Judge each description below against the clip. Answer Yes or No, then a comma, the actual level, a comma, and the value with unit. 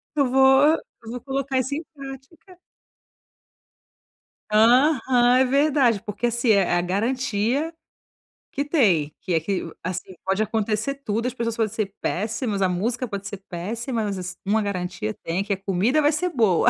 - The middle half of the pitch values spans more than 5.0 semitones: Yes, wide, 5.4 semitones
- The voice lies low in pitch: No, high, 225 Hz